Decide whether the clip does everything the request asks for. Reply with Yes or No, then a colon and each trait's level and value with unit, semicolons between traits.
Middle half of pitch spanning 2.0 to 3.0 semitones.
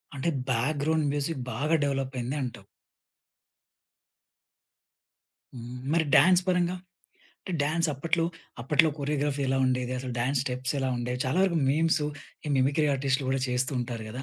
No: average, 3.6 semitones